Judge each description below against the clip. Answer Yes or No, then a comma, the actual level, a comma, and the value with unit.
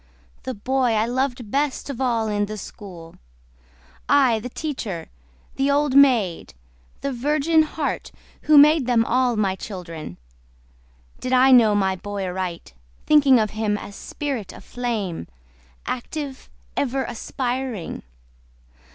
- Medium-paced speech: No, slow, 130 wpm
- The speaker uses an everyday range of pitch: Yes, average, 4.8 semitones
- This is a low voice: No, high, 245 Hz